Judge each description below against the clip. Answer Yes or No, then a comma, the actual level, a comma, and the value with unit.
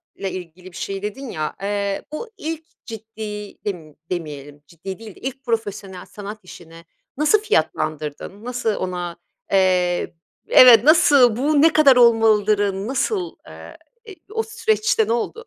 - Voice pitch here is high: Yes, high, 210 Hz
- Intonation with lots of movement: Yes, wide, 6.6 semitones